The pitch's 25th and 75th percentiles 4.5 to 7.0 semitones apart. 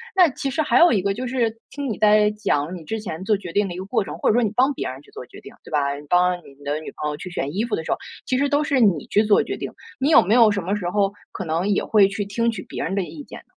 Yes: average, 4.8 semitones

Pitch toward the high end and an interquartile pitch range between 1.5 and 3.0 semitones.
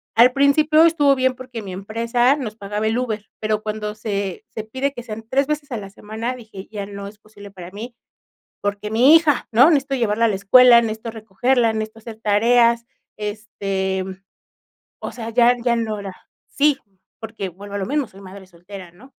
No: high, 220 Hz; average, 3.6 semitones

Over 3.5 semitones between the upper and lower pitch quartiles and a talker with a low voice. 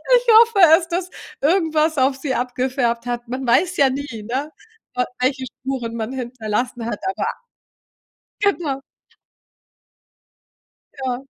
No: average, 4.2 semitones; very high, 265 Hz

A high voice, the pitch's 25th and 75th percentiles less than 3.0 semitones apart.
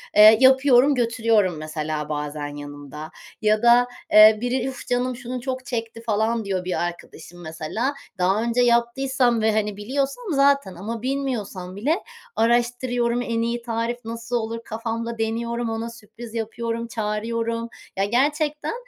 Yes: high, 230 Hz; narrow, 2.6 semitones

